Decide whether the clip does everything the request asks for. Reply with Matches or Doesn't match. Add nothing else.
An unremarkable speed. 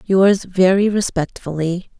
Doesn't match